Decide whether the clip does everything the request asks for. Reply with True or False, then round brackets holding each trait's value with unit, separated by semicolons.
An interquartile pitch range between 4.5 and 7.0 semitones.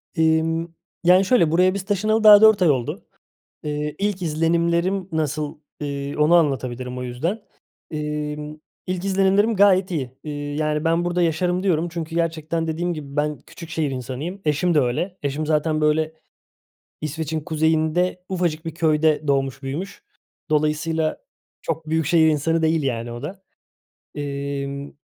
False (2.9 semitones)